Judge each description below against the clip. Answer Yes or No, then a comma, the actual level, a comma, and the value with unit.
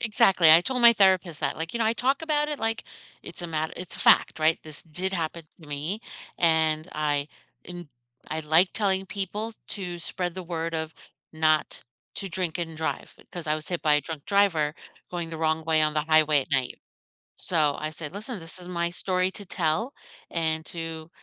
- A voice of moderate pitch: Yes, medium, 165 Hz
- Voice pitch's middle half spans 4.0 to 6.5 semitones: No, average, 3.3 semitones